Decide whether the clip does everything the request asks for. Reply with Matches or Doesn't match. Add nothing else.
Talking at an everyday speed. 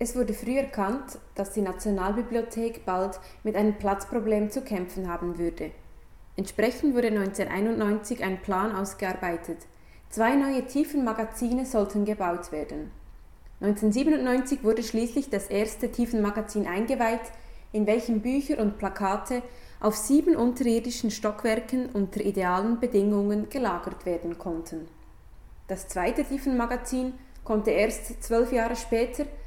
Doesn't match